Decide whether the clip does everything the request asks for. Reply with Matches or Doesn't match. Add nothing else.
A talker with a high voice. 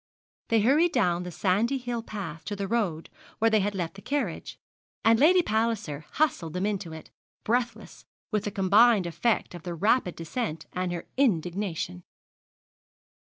Matches